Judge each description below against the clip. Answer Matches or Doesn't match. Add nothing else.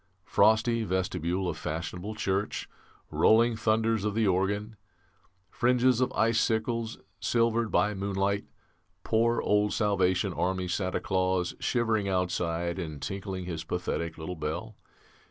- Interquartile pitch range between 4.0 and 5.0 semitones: Doesn't match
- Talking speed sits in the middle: Doesn't match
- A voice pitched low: Matches